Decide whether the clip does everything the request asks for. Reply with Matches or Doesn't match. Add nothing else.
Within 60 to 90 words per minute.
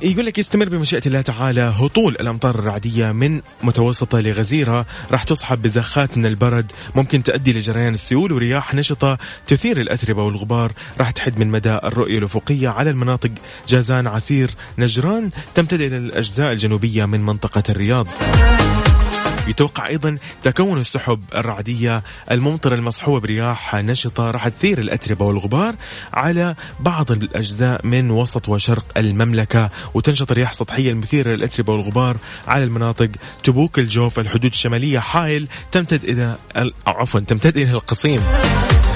Doesn't match